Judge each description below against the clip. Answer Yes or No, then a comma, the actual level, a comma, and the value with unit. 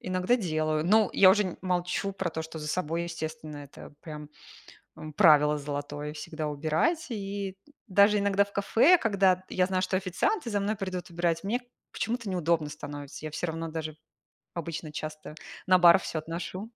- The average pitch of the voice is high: No, medium, 175 Hz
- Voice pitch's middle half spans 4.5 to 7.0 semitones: No, average, 4.1 semitones